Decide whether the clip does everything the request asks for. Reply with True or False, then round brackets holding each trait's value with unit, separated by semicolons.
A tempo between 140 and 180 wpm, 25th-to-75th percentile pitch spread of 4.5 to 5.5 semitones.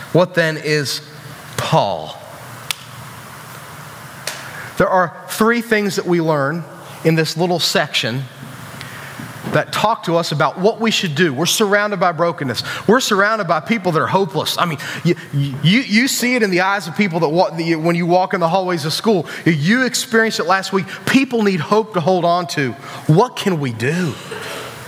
True (175 wpm; 5.1 semitones)